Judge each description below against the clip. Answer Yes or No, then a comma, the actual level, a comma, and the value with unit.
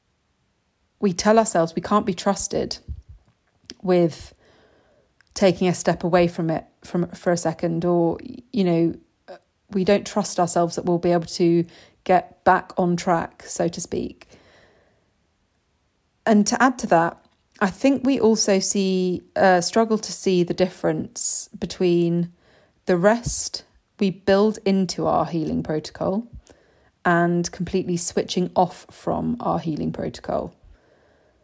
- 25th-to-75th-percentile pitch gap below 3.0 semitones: Yes, narrow, 2.6 semitones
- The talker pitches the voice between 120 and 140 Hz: No, medium, 180 Hz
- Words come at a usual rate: No, slow, 130 wpm